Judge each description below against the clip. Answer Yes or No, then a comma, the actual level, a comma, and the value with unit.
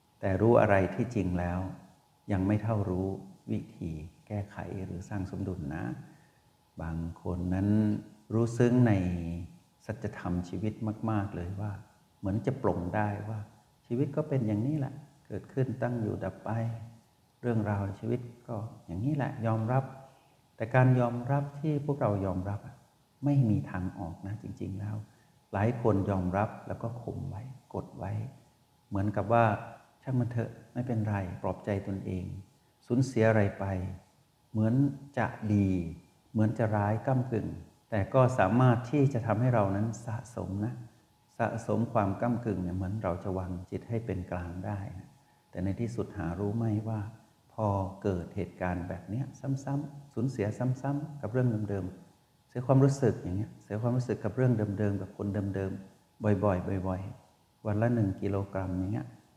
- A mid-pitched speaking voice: No, low, 105 Hz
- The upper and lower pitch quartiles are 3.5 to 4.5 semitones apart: Yes, average, 3.9 semitones